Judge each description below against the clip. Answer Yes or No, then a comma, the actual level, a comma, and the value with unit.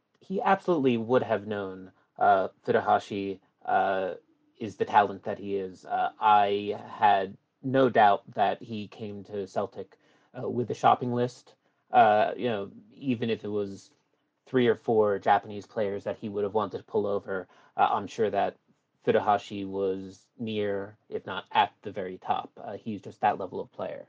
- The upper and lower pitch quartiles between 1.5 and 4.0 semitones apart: No, average, 4.4 semitones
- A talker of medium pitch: No, low, 105 Hz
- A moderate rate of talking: Yes, average, 170 wpm